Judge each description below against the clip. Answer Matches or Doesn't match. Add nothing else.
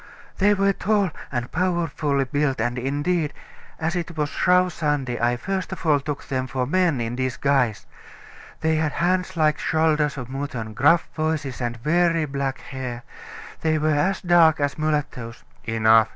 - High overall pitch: Doesn't match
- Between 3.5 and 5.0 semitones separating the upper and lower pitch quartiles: Matches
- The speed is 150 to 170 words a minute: Matches